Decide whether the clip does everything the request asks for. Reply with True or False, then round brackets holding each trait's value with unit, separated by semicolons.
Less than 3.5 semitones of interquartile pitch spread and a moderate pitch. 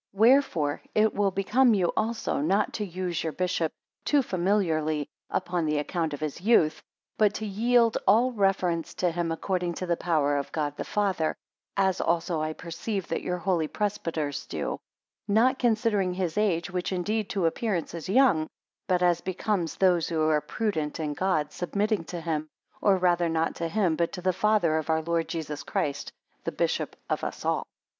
False (4.1 semitones; 180 Hz)